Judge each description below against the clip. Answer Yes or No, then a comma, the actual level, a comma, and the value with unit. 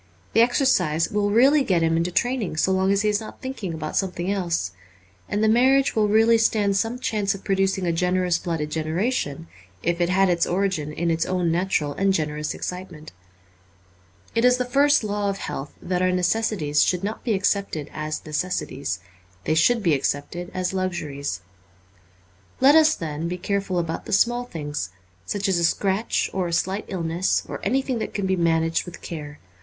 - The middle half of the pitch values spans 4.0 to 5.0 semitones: Yes, average, 4.3 semitones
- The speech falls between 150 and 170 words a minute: No, average, 185 wpm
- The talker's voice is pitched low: No, medium, 185 Hz